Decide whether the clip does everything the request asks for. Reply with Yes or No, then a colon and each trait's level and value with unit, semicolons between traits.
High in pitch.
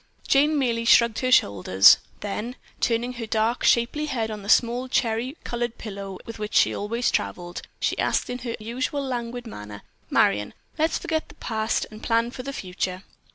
Yes: high, 230 Hz